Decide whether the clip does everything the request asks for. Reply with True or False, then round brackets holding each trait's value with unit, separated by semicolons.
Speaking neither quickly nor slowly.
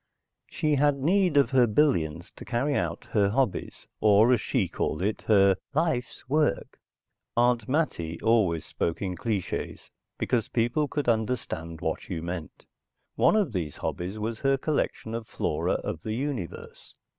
True (155 wpm)